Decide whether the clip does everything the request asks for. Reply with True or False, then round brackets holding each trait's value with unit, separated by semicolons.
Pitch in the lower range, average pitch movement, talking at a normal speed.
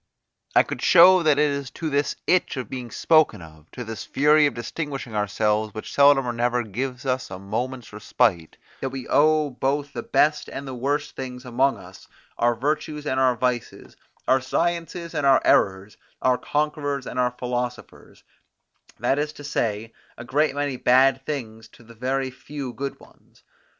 True (130 Hz; 3.3 semitones; 175 wpm)